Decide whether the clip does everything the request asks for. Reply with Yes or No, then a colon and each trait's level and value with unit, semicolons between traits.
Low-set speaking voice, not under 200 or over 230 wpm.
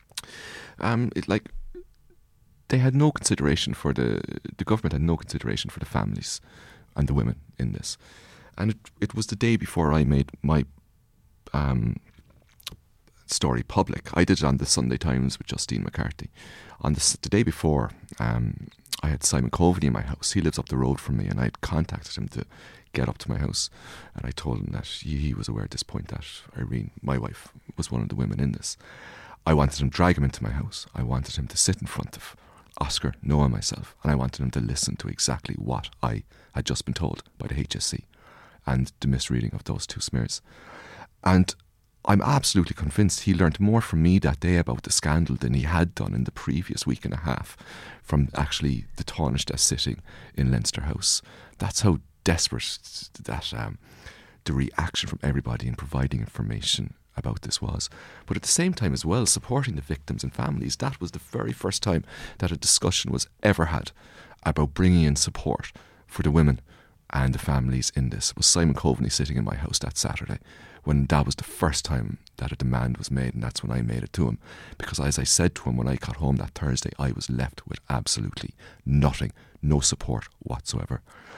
Yes: very low, 75 Hz; fast, 205 wpm